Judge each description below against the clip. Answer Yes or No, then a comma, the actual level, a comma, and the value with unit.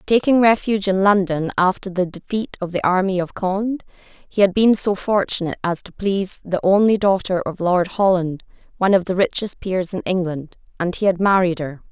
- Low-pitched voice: No, high, 190 Hz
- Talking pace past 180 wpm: Yes, average, 190 wpm